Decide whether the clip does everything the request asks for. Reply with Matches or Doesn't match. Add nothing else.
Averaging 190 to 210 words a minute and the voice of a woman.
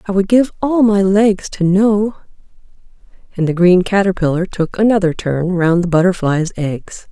Doesn't match